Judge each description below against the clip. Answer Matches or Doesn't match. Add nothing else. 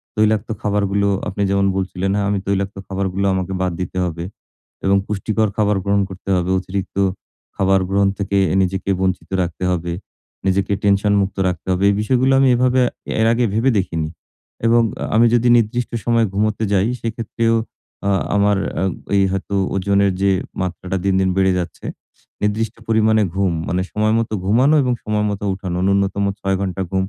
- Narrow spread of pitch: Matches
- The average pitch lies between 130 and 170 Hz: Doesn't match